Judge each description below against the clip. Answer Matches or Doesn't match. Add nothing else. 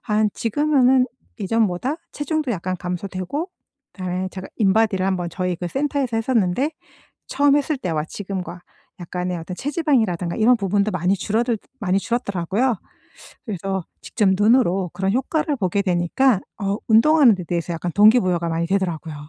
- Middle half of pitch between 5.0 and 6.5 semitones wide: Matches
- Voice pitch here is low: Doesn't match